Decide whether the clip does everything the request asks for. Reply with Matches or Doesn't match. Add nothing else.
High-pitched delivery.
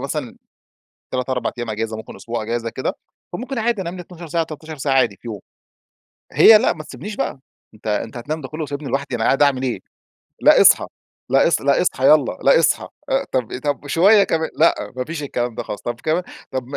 Doesn't match